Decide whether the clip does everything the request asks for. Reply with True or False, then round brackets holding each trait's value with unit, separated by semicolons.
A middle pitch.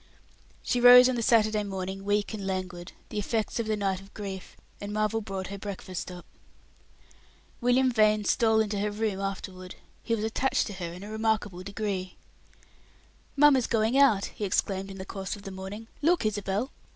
False (205 Hz)